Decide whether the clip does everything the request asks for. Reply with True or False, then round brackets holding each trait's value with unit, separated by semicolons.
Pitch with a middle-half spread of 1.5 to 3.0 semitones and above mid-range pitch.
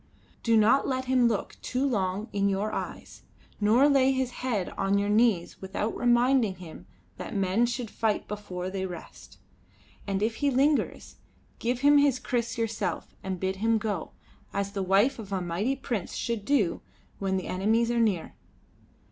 False (4.1 semitones; 215 Hz)